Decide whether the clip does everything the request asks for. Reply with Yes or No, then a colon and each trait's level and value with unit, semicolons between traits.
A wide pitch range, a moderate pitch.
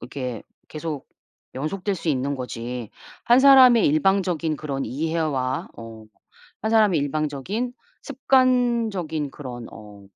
Yes: wide, 8.2 semitones; medium, 155 Hz